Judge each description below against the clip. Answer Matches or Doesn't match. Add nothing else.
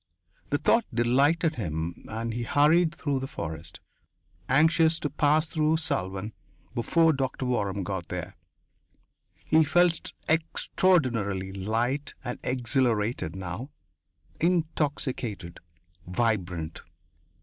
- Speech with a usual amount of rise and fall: Doesn't match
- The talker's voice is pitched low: Matches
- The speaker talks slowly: Matches